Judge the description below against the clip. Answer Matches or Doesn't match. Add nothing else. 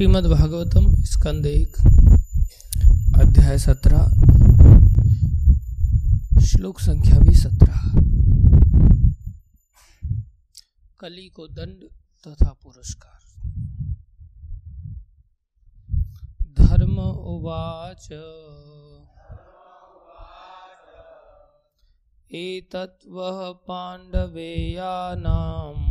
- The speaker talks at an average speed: Doesn't match